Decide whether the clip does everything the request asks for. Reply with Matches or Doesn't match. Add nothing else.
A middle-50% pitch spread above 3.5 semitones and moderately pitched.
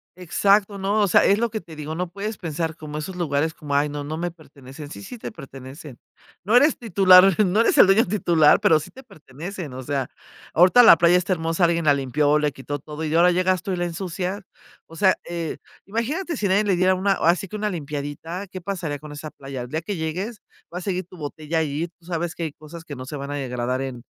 Matches